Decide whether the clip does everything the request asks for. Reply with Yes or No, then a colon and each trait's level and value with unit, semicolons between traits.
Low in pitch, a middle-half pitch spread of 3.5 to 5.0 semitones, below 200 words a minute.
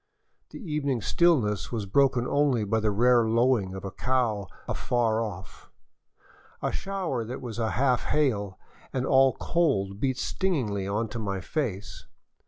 Yes: low, 120 Hz; average, 4.5 semitones; average, 140 wpm